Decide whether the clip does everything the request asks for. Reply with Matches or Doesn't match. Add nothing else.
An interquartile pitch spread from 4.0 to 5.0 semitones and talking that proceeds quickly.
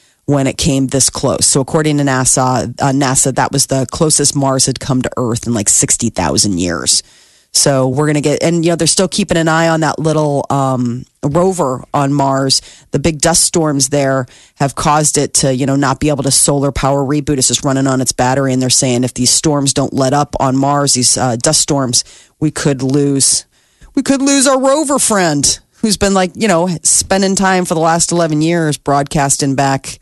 Doesn't match